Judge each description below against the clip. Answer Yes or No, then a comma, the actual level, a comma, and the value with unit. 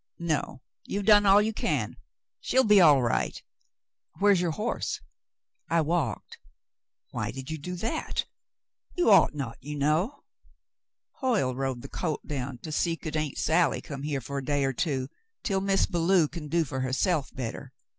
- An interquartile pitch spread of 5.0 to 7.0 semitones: Yes, wide, 5.6 semitones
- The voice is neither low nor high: Yes, medium, 155 Hz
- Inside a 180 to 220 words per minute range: No, average, 170 wpm